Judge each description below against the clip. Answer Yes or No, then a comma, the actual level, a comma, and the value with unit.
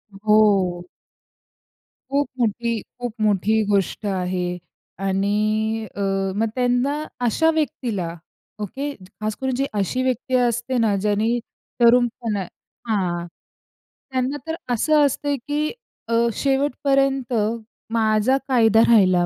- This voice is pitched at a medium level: No, high, 225 Hz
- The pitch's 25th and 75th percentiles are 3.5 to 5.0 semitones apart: Yes, average, 4.2 semitones